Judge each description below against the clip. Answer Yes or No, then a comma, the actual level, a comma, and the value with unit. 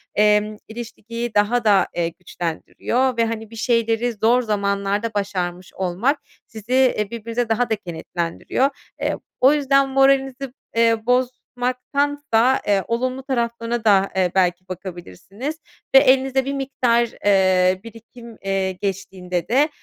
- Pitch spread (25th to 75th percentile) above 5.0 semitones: No, average, 4.4 semitones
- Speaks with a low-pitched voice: No, high, 230 Hz